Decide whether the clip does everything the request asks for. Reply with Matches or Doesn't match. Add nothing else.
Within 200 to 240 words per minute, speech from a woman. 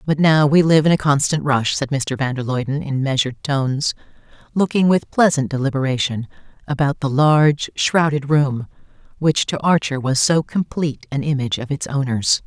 Doesn't match